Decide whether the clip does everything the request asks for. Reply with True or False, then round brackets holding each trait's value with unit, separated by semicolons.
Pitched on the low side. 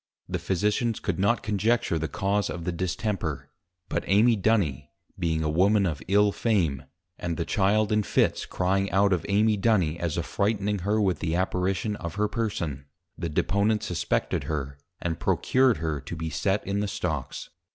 True (95 Hz)